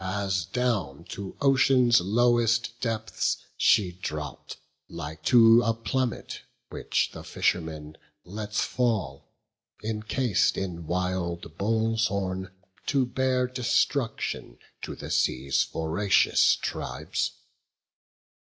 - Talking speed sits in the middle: No, slow, 100 wpm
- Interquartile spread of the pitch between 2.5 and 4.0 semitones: No, average, 5.2 semitones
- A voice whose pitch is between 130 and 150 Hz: No, low, 105 Hz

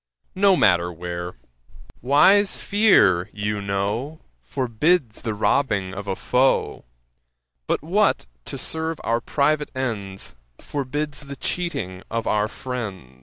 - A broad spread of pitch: Yes, wide, 7.3 semitones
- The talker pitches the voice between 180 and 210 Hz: No, low, 115 Hz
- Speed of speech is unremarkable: No, slow, 120 wpm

